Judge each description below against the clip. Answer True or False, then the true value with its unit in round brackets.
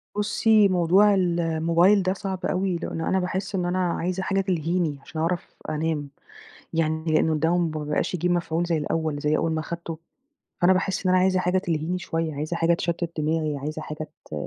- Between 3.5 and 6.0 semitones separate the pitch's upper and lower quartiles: False (2.6 semitones)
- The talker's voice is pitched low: False (170 Hz)